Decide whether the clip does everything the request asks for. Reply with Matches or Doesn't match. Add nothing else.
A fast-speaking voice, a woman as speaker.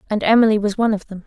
Matches